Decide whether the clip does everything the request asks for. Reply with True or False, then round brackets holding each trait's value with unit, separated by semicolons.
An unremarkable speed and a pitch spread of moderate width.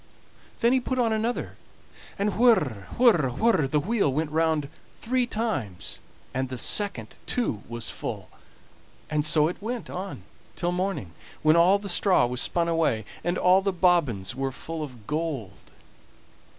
False (160 wpm; 7.3 semitones)